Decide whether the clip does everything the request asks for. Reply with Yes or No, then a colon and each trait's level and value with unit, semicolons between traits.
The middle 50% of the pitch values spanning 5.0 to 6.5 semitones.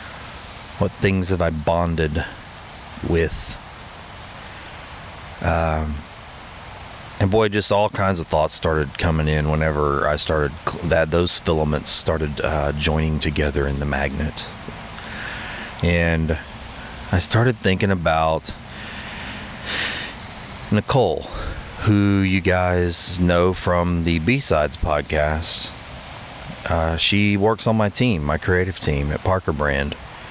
No: average, 3.8 semitones